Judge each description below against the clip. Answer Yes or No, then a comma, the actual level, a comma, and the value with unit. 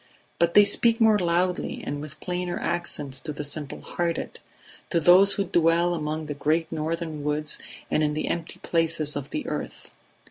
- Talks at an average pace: Yes, average, 175 wpm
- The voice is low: No, medium, 165 Hz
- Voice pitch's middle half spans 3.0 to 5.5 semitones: No, narrow, 2.6 semitones